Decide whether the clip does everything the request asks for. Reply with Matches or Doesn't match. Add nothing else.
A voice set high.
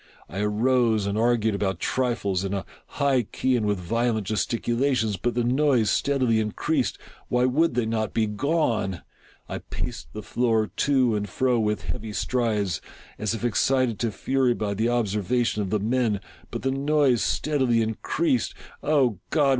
Doesn't match